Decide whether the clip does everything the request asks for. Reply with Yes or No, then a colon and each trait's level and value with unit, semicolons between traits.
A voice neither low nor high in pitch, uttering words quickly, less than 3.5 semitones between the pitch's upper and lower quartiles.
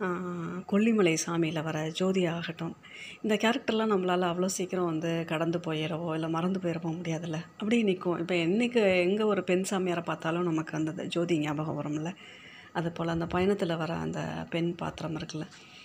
Yes: medium, 170 Hz; fast, 150 wpm; narrow, 2.5 semitones